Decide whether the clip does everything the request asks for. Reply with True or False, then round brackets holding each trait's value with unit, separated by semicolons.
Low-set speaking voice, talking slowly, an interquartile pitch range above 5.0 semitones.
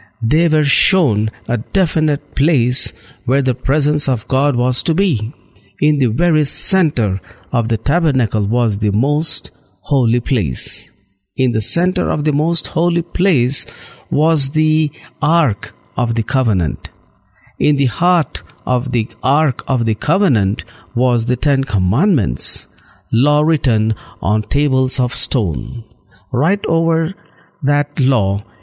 True (130 Hz; 130 wpm; 5.5 semitones)